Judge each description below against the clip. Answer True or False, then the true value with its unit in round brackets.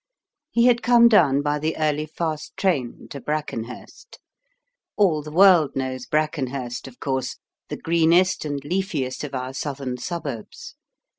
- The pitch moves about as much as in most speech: True (4.3 semitones)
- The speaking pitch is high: False (150 Hz)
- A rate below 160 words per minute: True (140 wpm)